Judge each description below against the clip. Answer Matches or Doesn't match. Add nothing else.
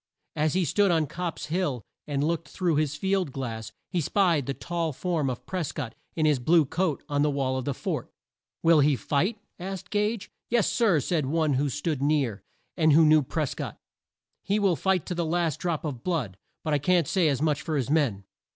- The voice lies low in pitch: Doesn't match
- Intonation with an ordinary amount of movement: Matches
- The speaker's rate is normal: Doesn't match